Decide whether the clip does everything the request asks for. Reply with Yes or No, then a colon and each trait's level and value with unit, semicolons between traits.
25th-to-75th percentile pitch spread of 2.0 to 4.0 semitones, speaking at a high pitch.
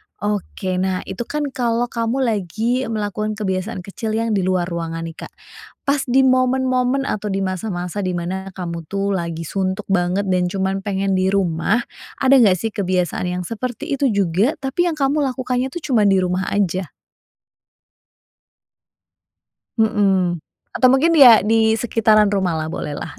No: average, 4.6 semitones; high, 200 Hz